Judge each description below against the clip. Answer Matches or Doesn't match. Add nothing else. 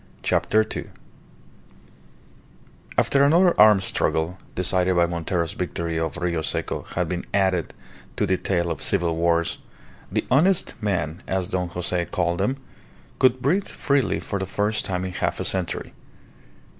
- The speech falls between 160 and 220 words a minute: Doesn't match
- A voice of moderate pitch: Doesn't match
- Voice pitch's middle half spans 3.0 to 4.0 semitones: Matches